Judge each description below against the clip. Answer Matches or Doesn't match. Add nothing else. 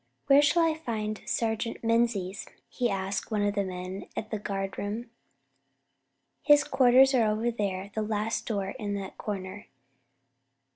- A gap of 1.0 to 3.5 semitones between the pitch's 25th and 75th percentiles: Matches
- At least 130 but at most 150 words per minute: Matches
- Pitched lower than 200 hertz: Doesn't match